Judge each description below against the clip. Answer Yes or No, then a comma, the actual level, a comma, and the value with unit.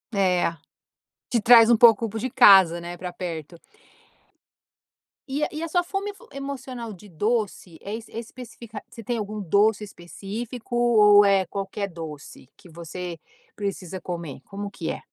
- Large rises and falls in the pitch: No, average, 4.7 semitones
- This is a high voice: Yes, high, 205 Hz